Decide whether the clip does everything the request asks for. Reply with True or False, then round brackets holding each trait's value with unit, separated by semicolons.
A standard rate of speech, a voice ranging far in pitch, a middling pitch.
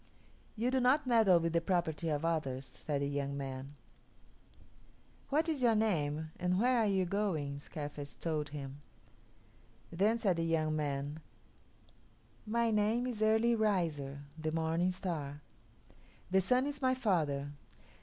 True (145 wpm; 7.0 semitones; 170 Hz)